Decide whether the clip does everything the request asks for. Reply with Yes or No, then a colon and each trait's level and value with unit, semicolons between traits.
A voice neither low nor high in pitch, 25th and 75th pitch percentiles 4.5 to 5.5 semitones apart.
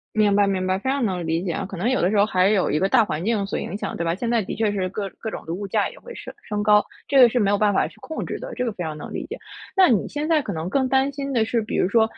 No: high, 210 Hz; average, 4.8 semitones